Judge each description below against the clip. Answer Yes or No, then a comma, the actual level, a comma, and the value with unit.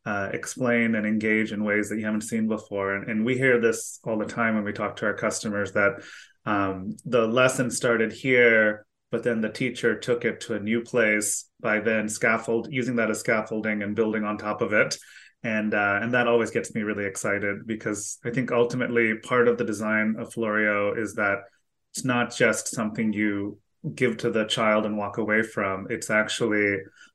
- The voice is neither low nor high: No, low, 110 Hz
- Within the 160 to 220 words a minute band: Yes, average, 200 wpm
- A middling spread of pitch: No, narrow, 2.0 semitones